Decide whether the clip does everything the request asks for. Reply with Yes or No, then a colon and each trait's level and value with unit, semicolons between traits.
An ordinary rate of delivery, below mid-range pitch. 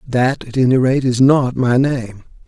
Yes: average, 195 wpm; low, 130 Hz